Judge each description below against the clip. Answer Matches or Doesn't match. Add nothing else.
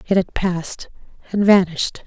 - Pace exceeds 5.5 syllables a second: Doesn't match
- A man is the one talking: Doesn't match